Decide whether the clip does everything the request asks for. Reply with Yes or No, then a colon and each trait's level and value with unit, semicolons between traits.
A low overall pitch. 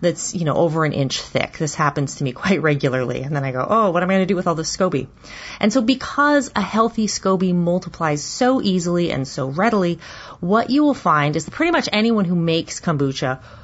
No: medium, 175 Hz